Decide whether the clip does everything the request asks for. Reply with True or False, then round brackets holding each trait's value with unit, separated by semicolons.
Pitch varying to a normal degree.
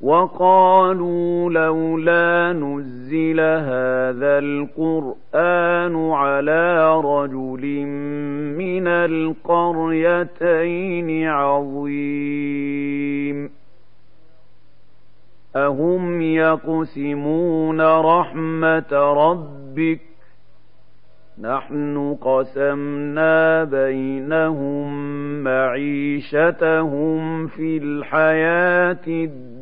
False (2.3 semitones)